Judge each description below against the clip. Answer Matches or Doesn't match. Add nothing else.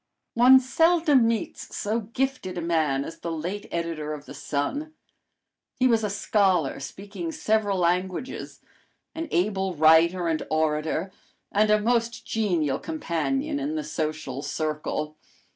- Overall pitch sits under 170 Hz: Doesn't match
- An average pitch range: Doesn't match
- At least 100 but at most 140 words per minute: Matches